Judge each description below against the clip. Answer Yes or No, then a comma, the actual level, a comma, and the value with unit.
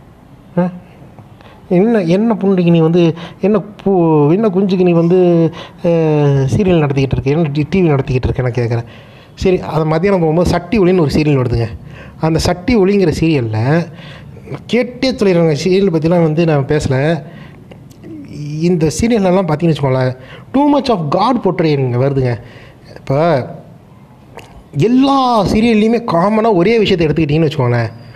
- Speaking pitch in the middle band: Yes, medium, 165 Hz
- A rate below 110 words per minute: No, average, 120 wpm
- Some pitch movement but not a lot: Yes, average, 5.0 semitones